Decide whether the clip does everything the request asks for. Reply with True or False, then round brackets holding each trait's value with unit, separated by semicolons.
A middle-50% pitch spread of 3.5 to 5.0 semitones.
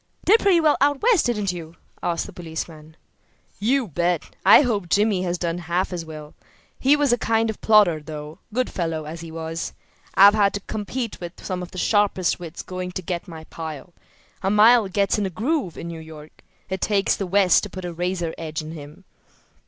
True (4.3 semitones)